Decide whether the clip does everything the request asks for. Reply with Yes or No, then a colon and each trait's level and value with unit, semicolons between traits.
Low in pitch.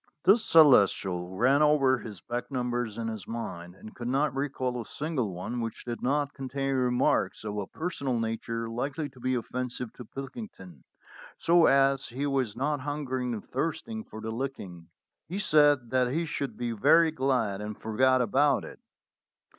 Yes: low, 125 Hz